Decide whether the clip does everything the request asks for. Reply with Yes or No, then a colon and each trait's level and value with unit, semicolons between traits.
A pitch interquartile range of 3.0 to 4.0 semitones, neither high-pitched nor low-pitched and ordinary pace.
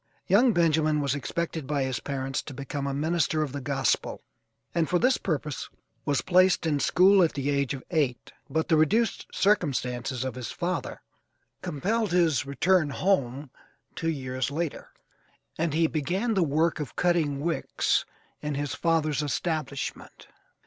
Yes: average, 3.6 semitones; medium, 155 Hz; average, 155 wpm